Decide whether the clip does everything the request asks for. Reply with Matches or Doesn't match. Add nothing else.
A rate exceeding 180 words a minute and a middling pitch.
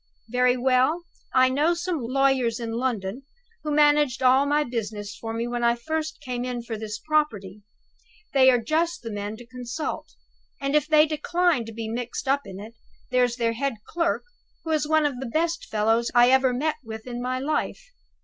Doesn't match